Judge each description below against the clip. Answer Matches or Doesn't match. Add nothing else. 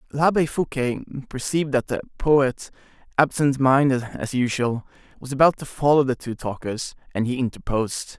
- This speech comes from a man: Matches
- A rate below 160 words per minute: Matches